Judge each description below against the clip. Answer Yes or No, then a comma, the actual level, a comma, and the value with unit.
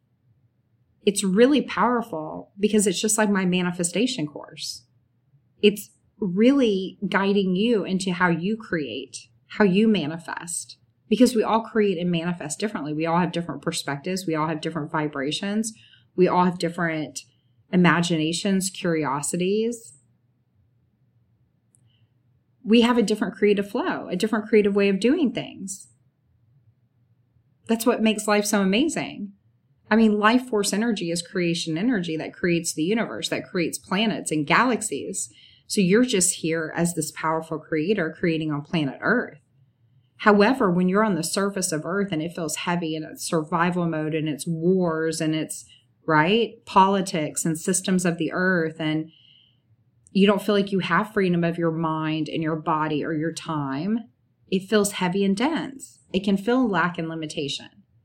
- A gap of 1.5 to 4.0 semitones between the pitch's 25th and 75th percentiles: No, average, 5.3 semitones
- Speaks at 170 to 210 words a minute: No, average, 155 wpm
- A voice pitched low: No, medium, 170 Hz